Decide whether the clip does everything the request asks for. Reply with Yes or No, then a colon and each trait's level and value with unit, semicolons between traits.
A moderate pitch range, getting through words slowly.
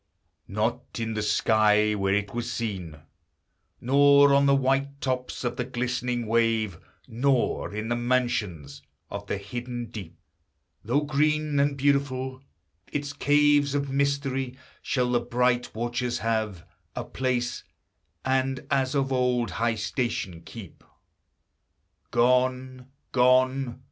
Yes: average, 3.0 semitones; slow, 125 wpm